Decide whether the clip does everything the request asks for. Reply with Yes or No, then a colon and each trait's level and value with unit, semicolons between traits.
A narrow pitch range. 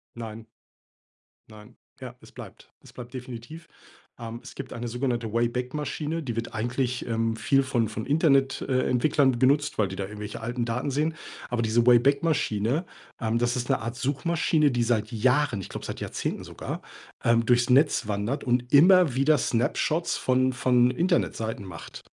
No: average, 3.2 semitones